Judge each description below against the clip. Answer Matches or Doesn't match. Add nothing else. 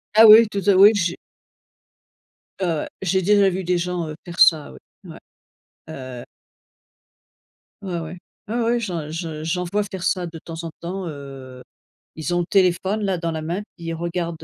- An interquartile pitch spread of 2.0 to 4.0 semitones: Matches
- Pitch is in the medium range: Matches